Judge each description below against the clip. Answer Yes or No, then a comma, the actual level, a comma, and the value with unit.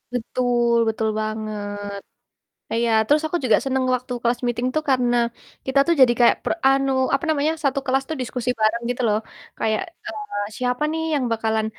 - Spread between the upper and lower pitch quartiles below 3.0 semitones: No, average, 3.3 semitones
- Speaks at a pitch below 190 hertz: No, high, 245 Hz